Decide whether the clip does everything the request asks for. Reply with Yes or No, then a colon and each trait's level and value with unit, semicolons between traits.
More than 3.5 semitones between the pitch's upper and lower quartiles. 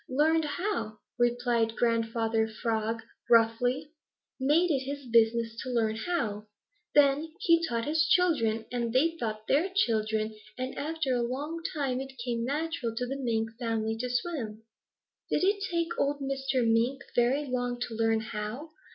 Yes: average, 4.3 semitones